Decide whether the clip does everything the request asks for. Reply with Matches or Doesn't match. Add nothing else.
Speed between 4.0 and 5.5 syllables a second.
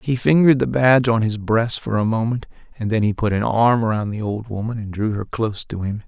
Doesn't match